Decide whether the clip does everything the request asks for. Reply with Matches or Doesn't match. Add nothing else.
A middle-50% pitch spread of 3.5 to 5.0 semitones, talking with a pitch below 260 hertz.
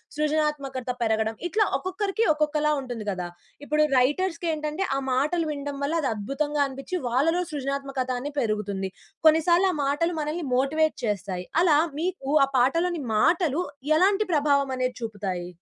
Doesn't match